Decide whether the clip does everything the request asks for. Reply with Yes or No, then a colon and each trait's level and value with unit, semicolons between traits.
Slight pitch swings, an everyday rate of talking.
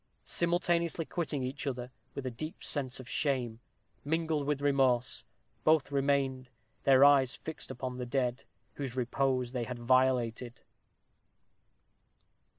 No: narrow, 2.3 semitones; slow, 125 wpm